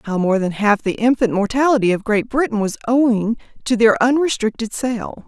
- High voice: Yes, high, 225 Hz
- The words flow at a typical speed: Yes, average, 180 wpm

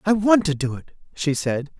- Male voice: Yes, male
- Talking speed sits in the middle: No, fast, 235 wpm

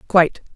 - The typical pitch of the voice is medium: Yes, medium, 175 Hz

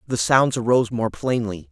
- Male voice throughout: Yes, male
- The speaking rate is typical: Yes, average, 175 wpm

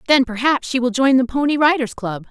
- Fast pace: Yes, fast, 235 wpm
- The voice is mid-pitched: No, very high, 255 Hz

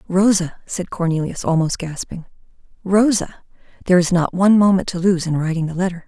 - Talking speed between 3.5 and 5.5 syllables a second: No, 5.8 syllables/s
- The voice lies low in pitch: No, medium, 180 Hz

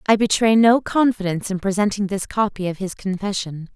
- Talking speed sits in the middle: Yes, average, 175 wpm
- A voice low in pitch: No, high, 200 Hz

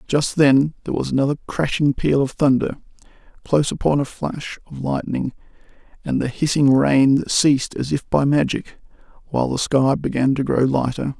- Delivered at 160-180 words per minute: Yes, average, 165 wpm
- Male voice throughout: Yes, male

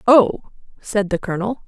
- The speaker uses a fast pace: No, average, 145 wpm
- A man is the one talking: No, female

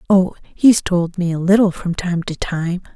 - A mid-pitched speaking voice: Yes, medium, 180 Hz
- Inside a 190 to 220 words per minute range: Yes, fast, 205 wpm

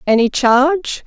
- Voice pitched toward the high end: Yes, very high, 270 Hz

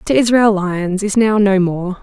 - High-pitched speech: Yes, high, 200 Hz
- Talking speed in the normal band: No, fast, 210 wpm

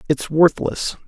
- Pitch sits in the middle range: Yes, medium, 155 Hz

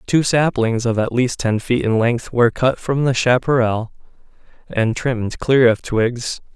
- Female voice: No, male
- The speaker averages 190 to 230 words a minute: No, average, 175 wpm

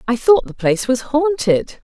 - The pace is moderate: Yes, average, 190 wpm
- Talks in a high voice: Yes, very high, 260 Hz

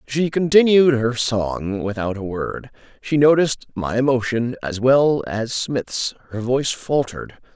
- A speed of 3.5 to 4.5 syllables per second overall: Yes, 4.2 syllables/s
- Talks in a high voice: No, low, 125 Hz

